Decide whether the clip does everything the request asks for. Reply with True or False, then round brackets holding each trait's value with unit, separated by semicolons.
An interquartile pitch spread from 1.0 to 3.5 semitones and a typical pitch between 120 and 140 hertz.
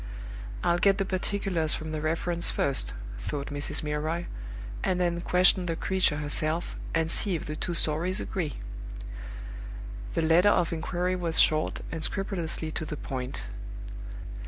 False (2.6 semitones; 165 Hz)